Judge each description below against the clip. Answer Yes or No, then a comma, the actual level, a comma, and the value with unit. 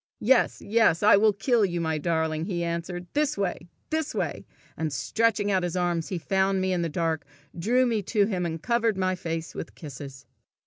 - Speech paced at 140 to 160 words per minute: No, average, 200 wpm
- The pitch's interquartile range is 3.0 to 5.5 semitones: Yes, average, 4.2 semitones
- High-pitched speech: No, medium, 180 Hz